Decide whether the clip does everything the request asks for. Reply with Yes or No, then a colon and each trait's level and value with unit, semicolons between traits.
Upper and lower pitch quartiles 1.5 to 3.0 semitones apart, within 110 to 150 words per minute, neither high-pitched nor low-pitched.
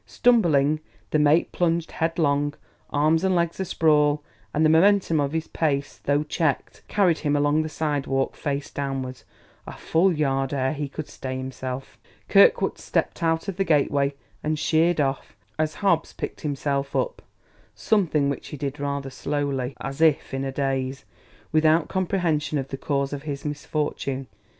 No: average, 2.7 semitones; average, 160 wpm; medium, 150 Hz